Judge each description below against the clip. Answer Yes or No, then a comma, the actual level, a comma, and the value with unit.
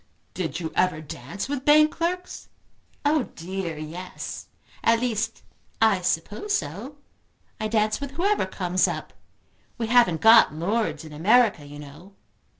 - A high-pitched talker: Yes, high, 205 Hz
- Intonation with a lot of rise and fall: Yes, wide, 6.9 semitones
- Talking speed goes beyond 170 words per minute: No, average, 140 wpm